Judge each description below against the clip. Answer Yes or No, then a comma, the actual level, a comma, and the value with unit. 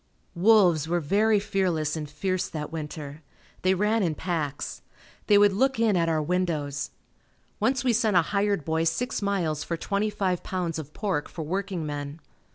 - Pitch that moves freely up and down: No, average, 4.6 semitones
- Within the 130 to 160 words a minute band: No, average, 170 wpm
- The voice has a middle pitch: Yes, medium, 180 Hz